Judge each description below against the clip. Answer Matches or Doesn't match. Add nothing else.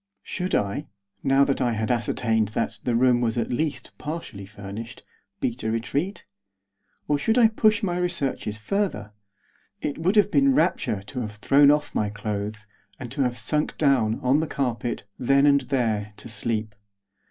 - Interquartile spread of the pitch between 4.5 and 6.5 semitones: Matches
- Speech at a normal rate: Matches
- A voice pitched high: Doesn't match